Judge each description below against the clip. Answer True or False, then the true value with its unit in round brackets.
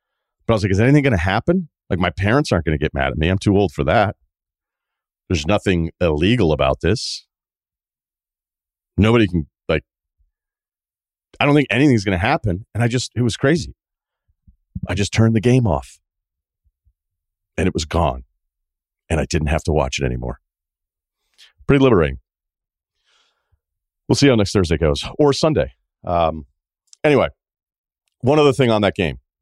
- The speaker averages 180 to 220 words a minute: False (155 wpm)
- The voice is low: True (85 Hz)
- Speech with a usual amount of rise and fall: False (6.5 semitones)